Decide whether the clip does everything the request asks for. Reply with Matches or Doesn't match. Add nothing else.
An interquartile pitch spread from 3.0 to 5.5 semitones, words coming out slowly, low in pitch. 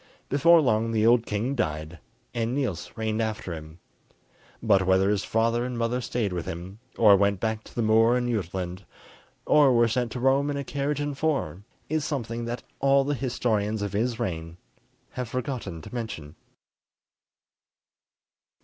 Doesn't match